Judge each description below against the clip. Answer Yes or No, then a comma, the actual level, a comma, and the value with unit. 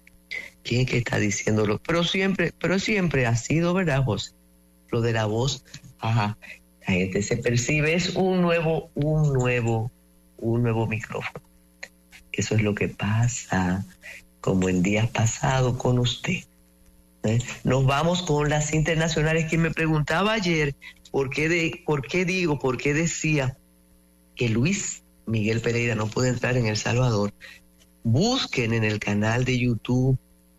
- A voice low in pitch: Yes, low, 120 Hz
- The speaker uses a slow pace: No, average, 150 wpm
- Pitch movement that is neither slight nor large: No, wide, 6.8 semitones